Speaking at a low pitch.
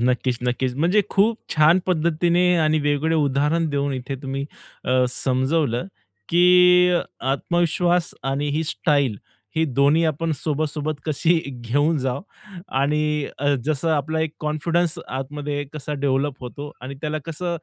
No: medium, 150 Hz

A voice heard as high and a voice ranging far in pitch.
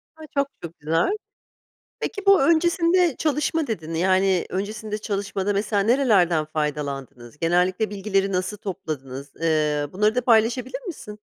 Yes: high, 200 Hz; wide, 7.1 semitones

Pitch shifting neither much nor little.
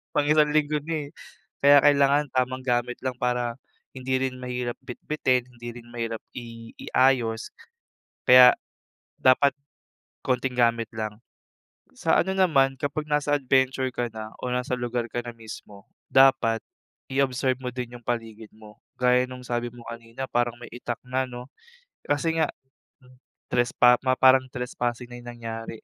No: narrow, 1.9 semitones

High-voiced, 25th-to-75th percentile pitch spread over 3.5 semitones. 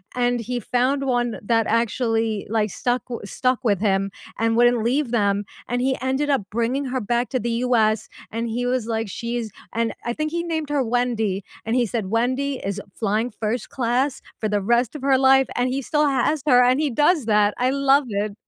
No: high, 240 Hz; average, 2.8 semitones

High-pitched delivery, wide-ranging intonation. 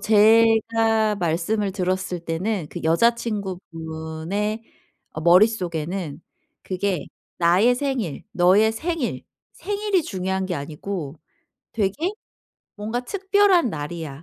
No: high, 195 Hz; average, 4.9 semitones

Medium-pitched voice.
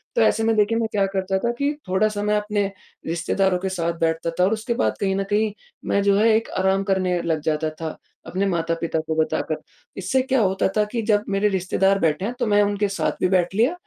No: high, 195 Hz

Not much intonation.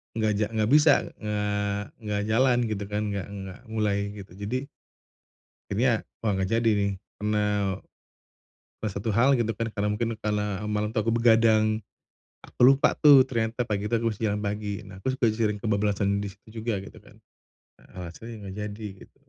Yes: narrow, 1.9 semitones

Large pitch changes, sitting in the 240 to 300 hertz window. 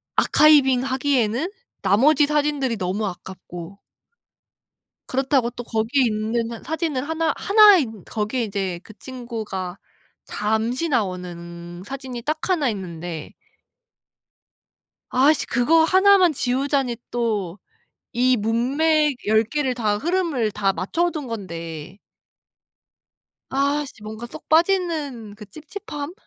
Yes: wide, 5.9 semitones; high, 245 Hz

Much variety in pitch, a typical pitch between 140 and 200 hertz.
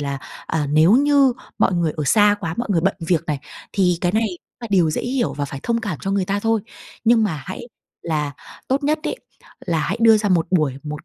Yes: wide, 6.0 semitones; medium, 185 Hz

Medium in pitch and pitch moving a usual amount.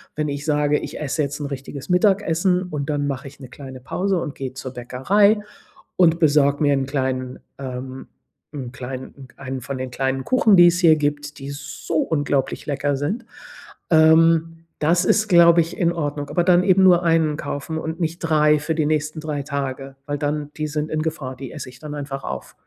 Yes: medium, 150 Hz; average, 3.2 semitones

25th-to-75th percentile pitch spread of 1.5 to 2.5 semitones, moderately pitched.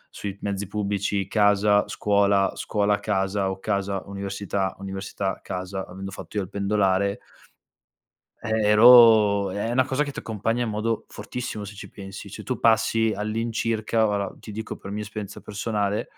No: narrow, 1.8 semitones; low, 105 Hz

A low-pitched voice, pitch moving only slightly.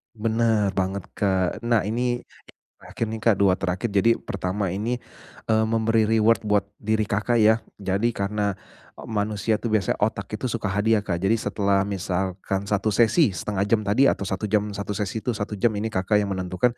Yes: low, 105 Hz; narrow, 2.2 semitones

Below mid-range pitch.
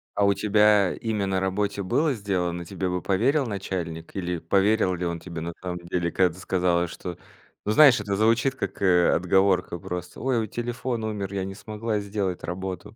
Yes: very low, 95 Hz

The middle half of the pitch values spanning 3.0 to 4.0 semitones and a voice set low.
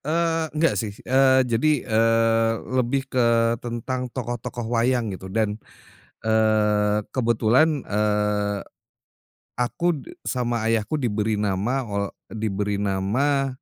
Yes: average, 3.6 semitones; low, 115 Hz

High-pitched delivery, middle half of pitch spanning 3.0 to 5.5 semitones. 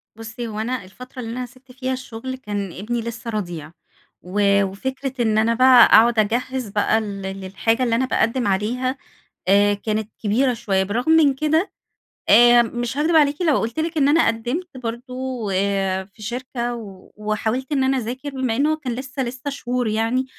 Yes: high, 240 Hz; average, 3.5 semitones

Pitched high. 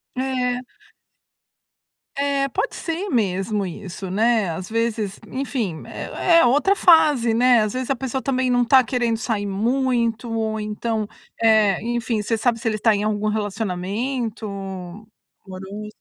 Yes: high, 230 Hz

